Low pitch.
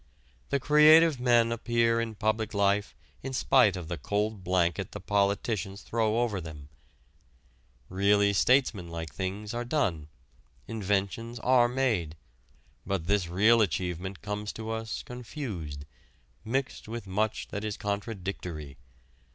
Yes: low, 105 Hz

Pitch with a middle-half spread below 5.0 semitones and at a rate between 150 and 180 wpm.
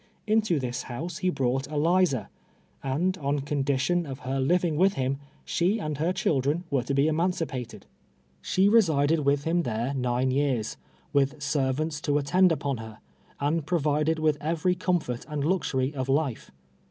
Yes: average, 4.1 semitones; average, 155 wpm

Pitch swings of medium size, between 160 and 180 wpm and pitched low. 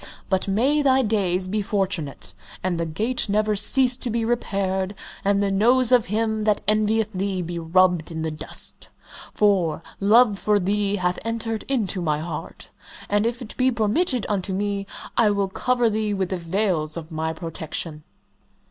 No: average, 3.6 semitones; average, 170 wpm; high, 200 Hz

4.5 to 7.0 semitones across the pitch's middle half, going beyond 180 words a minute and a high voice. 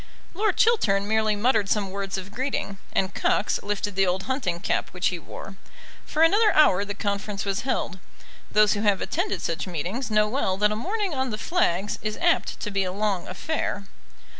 Yes: average, 5.0 semitones; average, 190 wpm; high, 205 Hz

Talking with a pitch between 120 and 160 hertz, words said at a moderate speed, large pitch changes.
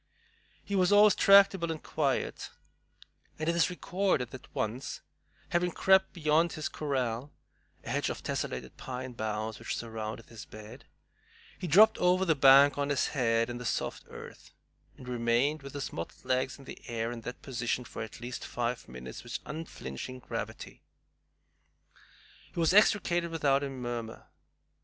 Yes: low, 135 Hz; average, 155 wpm; wide, 6.0 semitones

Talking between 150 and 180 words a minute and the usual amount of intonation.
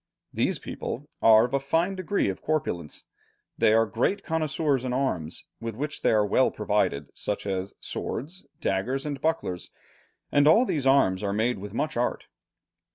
No: average, 165 wpm; wide, 6.7 semitones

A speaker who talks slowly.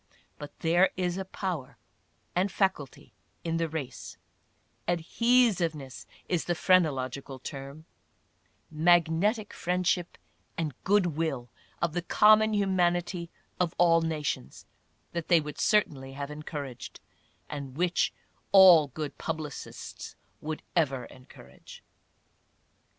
Yes: slow, 115 wpm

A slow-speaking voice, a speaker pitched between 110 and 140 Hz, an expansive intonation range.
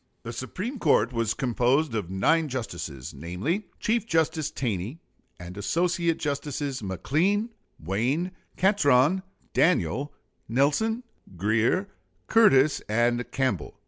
Yes: slow, 105 wpm; low, 135 Hz; wide, 7.1 semitones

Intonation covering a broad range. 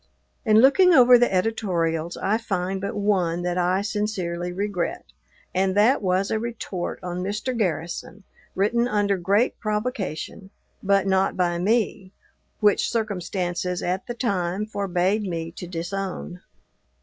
No: average, 3.2 semitones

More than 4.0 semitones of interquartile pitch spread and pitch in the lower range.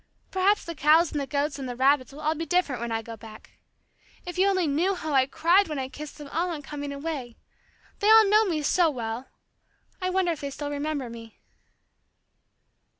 No: average, 4.6 semitones; very high, 295 Hz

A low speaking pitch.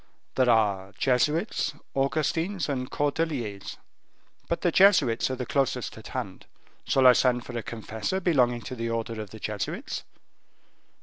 Yes: low, 125 Hz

